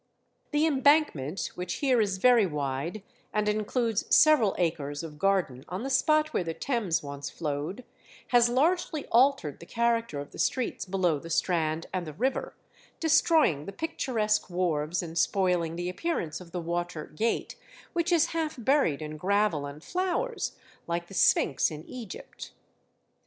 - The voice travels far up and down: Yes, wide, 8.0 semitones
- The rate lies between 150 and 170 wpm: Yes, average, 155 wpm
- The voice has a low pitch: No, high, 190 Hz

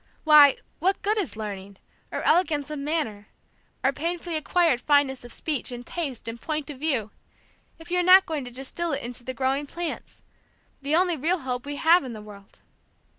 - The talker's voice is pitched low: No, very high, 290 Hz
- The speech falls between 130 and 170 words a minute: No, average, 190 wpm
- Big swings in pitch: No, average, 5.0 semitones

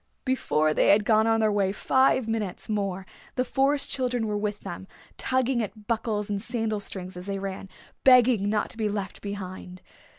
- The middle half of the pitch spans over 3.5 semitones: No, average, 3.0 semitones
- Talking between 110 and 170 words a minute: No, average, 190 wpm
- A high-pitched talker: Yes, high, 210 Hz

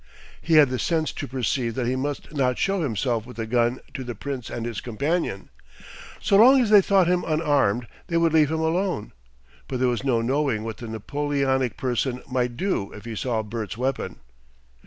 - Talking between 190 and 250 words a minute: Yes, average, 200 wpm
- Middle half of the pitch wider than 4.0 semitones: Yes, average, 4.9 semitones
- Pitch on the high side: No, low, 130 Hz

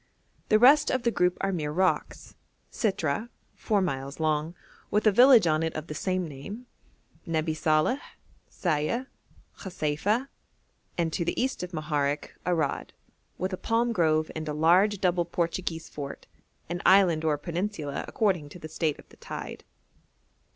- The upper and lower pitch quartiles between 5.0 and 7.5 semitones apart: No, average, 4.4 semitones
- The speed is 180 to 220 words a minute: No, average, 160 wpm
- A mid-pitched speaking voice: Yes, medium, 170 Hz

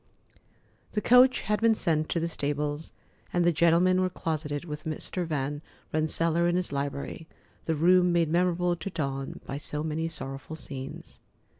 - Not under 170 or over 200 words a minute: No, average, 160 wpm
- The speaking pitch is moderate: Yes, medium, 160 Hz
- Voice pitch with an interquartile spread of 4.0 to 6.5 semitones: No, average, 3.0 semitones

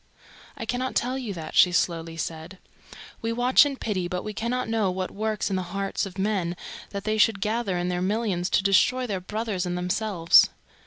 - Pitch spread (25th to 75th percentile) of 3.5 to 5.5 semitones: Yes, average, 3.8 semitones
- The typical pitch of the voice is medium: No, high, 195 Hz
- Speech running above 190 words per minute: Yes, average, 200 wpm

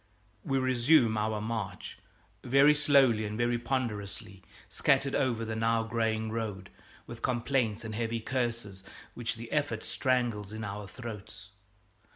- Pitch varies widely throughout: No, average, 3.0 semitones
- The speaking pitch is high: No, low, 115 Hz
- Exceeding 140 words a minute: No, slow, 135 wpm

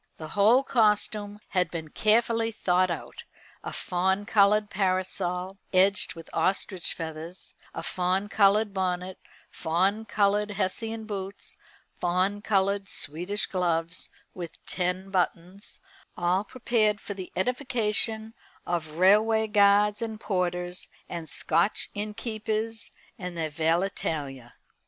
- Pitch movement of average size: Yes, average, 3.0 semitones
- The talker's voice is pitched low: No, high, 195 Hz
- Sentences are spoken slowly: Yes, slow, 115 wpm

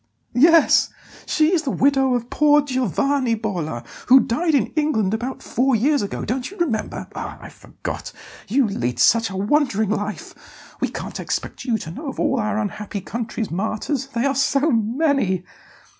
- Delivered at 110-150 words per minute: No, average, 170 wpm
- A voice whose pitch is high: Yes, high, 245 Hz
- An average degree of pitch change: Yes, average, 4.8 semitones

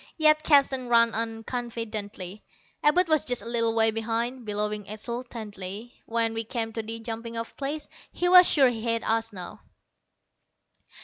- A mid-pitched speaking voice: No, high, 230 Hz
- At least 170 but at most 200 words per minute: No, average, 160 wpm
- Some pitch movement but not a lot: No, narrow, 1.9 semitones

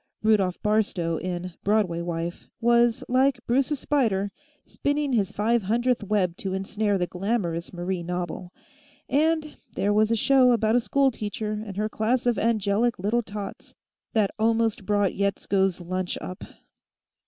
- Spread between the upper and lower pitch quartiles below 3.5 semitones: No, average, 3.9 semitones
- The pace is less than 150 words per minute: Yes, average, 140 wpm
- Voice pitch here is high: Yes, high, 210 Hz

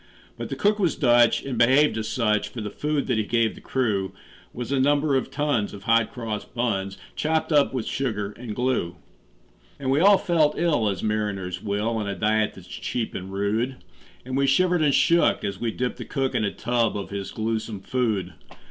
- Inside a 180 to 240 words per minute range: Yes, fast, 205 wpm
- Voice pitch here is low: Yes, low, 115 Hz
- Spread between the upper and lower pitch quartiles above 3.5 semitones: Yes, average, 4.6 semitones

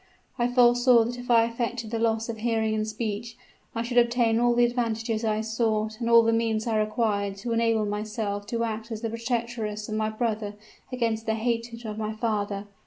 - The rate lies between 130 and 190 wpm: No, average, 200 wpm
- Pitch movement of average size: No, narrow, 1.4 semitones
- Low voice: No, high, 225 Hz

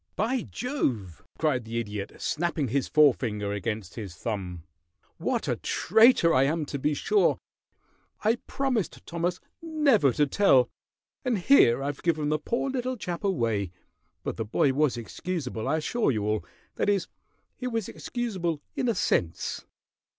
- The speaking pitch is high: No, medium, 150 Hz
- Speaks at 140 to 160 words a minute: Yes, average, 150 wpm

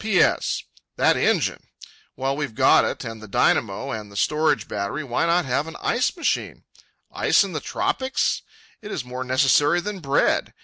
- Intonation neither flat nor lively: No, wide, 6.2 semitones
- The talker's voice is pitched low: No, medium, 145 Hz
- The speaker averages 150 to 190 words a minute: Yes, average, 165 wpm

